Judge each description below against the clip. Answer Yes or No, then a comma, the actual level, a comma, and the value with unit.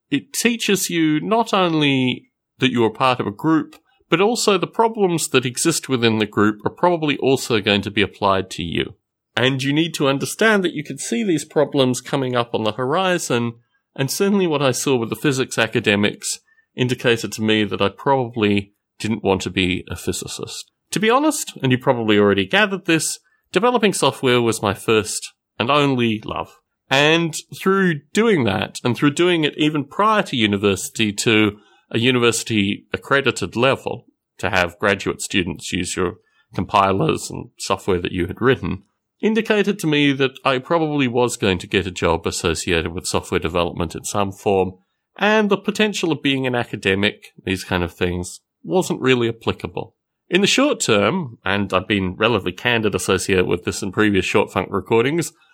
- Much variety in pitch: Yes, wide, 7.6 semitones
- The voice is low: Yes, low, 125 Hz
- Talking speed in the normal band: Yes, average, 175 wpm